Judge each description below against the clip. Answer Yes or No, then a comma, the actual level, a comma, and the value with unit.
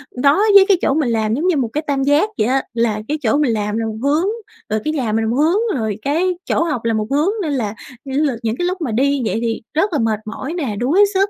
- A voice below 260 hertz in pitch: No, very high, 275 Hz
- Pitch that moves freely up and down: Yes, wide, 5.9 semitones